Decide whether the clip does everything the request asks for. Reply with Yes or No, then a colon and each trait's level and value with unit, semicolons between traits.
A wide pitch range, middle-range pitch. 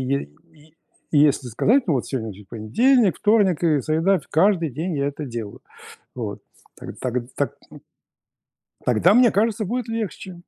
Yes: wide, 8.3 semitones; medium, 160 Hz